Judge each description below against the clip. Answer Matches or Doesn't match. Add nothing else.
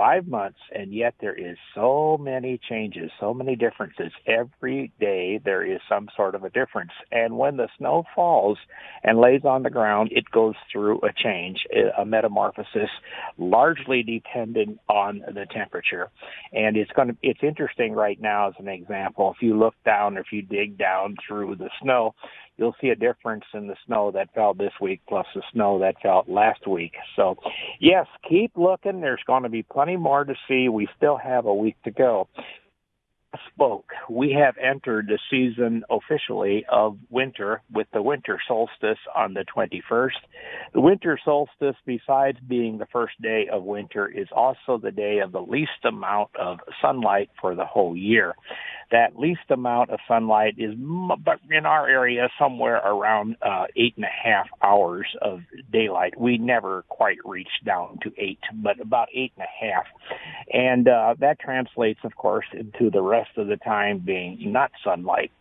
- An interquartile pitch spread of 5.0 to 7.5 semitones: Doesn't match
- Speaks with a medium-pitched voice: Doesn't match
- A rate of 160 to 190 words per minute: Matches